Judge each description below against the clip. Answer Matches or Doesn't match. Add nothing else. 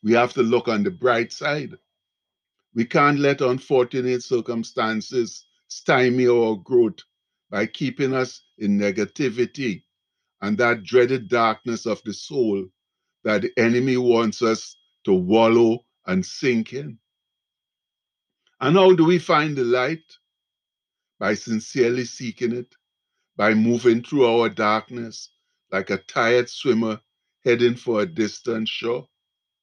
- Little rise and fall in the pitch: Matches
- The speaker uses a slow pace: Matches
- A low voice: Matches